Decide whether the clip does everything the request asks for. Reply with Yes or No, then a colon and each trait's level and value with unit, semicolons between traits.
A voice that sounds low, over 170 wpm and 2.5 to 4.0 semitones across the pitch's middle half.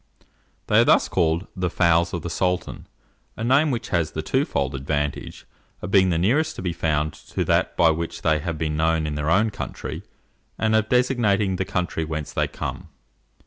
No: very low, 85 Hz; average, 190 wpm; average, 4.4 semitones